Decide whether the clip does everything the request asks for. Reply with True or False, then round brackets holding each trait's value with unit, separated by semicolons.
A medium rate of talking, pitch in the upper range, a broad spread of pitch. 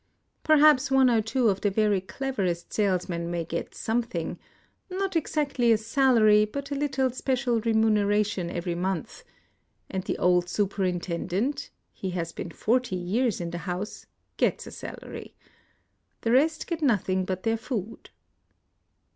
True (155 wpm; 215 Hz; 6.0 semitones)